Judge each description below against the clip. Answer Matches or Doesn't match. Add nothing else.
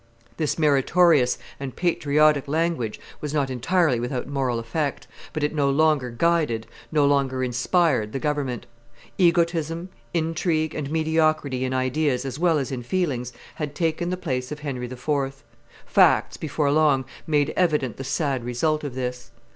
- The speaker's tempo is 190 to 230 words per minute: Doesn't match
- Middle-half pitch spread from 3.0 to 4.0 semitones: Matches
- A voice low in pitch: Doesn't match